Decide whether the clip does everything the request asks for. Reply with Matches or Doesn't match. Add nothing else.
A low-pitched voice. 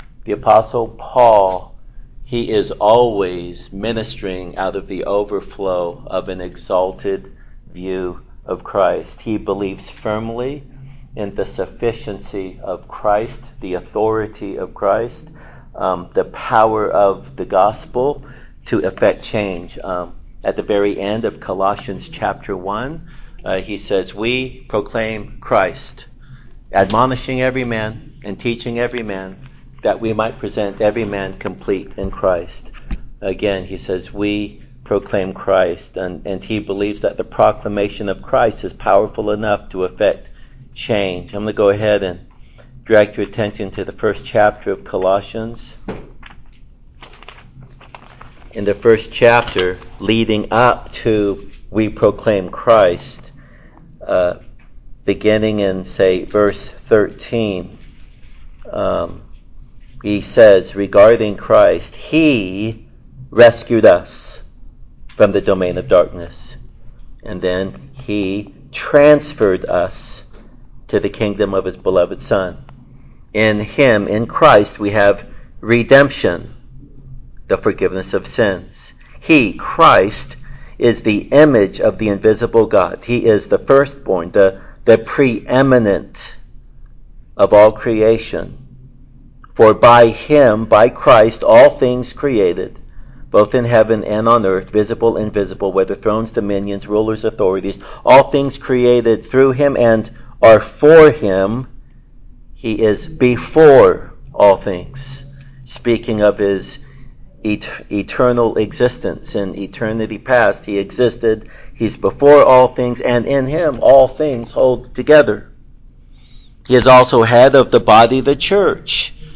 Matches